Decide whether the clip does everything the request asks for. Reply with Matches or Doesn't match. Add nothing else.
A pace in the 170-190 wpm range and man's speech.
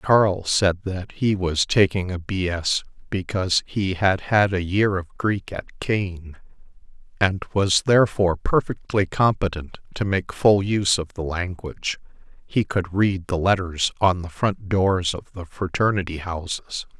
Doesn't match